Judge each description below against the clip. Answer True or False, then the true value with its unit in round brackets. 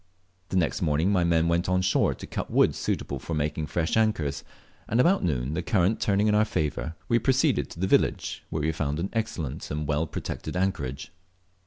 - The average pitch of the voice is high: False (85 Hz)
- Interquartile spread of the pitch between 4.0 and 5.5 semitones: True (4.7 semitones)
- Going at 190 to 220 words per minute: True (200 wpm)